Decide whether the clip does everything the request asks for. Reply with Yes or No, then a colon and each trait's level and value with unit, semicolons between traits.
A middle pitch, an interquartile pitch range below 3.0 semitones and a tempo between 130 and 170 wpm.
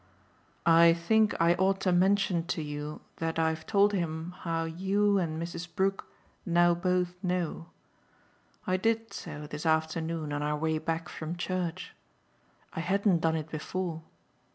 Yes: medium, 170 Hz; narrow, 2.5 semitones; average, 150 wpm